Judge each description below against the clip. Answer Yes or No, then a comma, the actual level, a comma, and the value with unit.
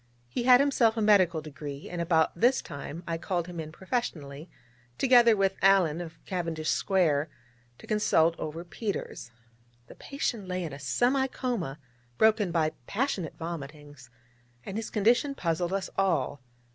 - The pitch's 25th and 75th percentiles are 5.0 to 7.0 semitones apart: Yes, wide, 5.6 semitones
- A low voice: No, medium, 175 Hz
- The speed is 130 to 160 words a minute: Yes, average, 150 wpm